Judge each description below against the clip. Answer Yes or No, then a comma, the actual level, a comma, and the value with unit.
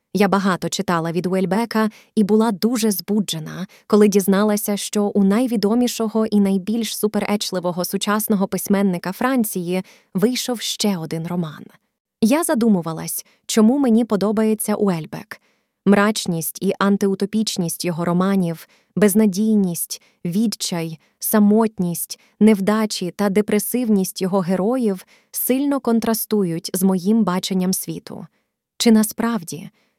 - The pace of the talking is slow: Yes, slow, 100 wpm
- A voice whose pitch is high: Yes, high, 205 Hz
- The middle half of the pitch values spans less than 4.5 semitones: Yes, average, 2.8 semitones